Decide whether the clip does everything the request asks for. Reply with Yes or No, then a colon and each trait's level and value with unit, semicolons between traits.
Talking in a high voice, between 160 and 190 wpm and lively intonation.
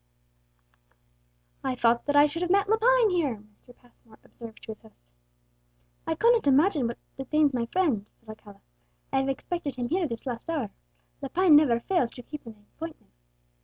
Yes: very high, 270 Hz; average, 170 wpm; wide, 6.2 semitones